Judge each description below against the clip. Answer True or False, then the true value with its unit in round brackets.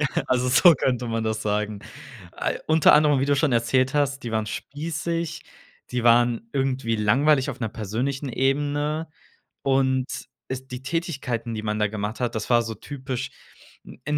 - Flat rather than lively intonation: False (3.8 semitones)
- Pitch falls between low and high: False (130 Hz)